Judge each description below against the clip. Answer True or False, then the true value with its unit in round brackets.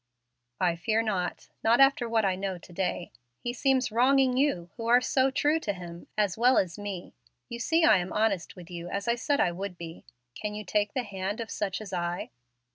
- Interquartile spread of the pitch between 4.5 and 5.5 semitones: True (5.0 semitones)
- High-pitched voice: True (210 Hz)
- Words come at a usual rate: False (215 wpm)